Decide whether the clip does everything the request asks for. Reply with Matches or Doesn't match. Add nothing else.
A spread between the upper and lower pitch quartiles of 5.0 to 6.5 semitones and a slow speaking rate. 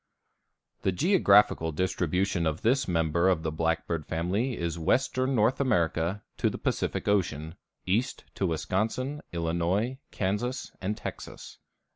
Matches